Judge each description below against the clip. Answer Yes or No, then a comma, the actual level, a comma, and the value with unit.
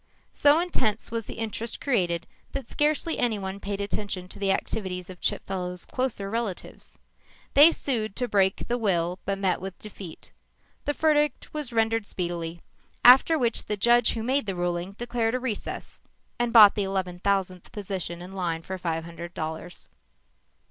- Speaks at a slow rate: No, average, 160 wpm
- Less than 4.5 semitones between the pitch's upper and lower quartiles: No, average, 4.8 semitones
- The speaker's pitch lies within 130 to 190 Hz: No, high, 200 Hz